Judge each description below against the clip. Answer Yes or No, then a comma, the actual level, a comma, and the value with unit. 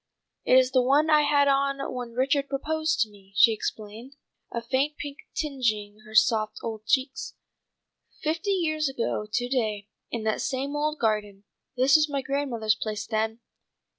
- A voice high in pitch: Yes, very high, 255 Hz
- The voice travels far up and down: No, average, 4.7 semitones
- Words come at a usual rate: Yes, average, 165 wpm